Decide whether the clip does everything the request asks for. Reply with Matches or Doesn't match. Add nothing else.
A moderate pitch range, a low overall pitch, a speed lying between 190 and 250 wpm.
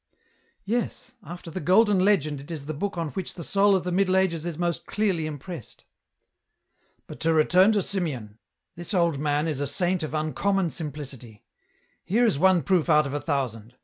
Doesn't match